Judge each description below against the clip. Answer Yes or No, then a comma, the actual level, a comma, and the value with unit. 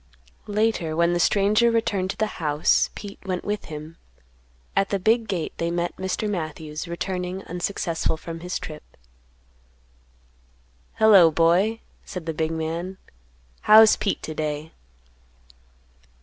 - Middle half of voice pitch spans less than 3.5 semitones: No, average, 3.9 semitones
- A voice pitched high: No, medium, 180 Hz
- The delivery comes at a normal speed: No, slow, 130 wpm